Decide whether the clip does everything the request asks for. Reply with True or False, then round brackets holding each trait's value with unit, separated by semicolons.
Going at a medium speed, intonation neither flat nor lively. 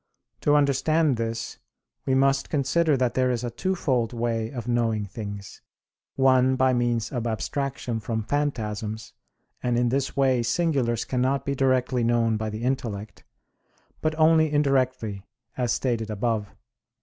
True (145 wpm; 3.2 semitones)